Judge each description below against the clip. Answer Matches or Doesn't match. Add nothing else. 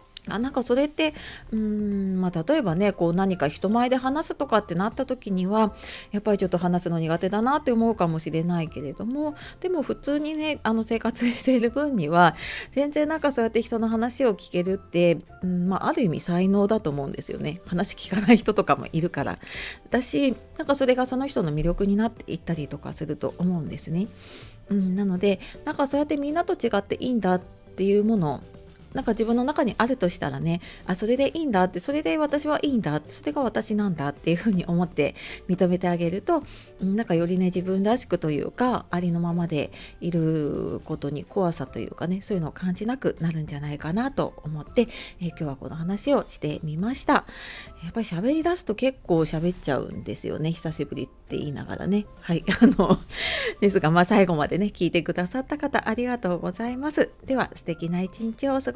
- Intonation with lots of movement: Matches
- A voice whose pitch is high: Matches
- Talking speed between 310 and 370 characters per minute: Doesn't match